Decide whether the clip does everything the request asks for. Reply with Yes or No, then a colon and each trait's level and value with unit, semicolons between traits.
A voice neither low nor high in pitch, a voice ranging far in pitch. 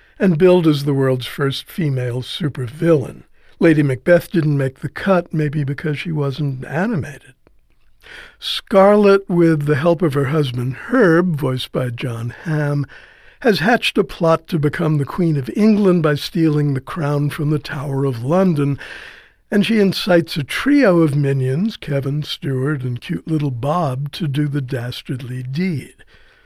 No: medium, 150 Hz; average, 3.9 semitones